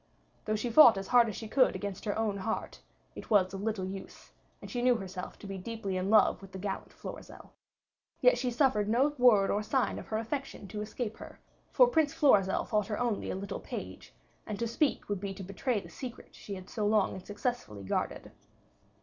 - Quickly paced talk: Yes, fast, 215 wpm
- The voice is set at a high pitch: Yes, high, 215 Hz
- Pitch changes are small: No, average, 3.7 semitones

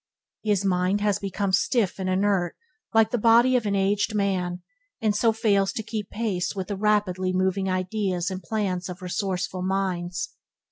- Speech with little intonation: Yes, narrow, 2.3 semitones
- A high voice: Yes, high, 195 Hz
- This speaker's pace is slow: No, average, 170 wpm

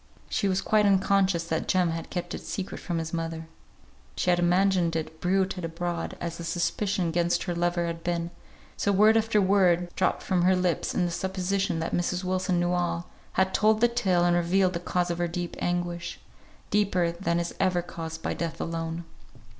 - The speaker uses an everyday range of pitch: No, narrow, 1.8 semitones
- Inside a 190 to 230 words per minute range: Yes, average, 195 wpm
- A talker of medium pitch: Yes, medium, 175 Hz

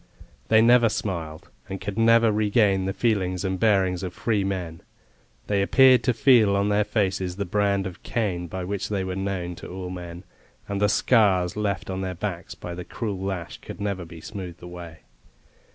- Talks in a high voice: No, very low, 95 Hz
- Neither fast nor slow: Yes, average, 185 wpm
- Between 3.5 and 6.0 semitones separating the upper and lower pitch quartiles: No, narrow, 2.6 semitones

